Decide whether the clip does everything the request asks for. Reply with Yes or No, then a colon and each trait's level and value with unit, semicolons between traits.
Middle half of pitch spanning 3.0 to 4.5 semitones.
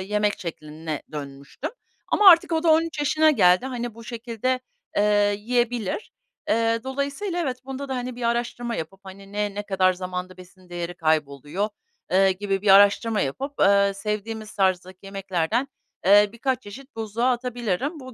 No: average, 5.0 semitones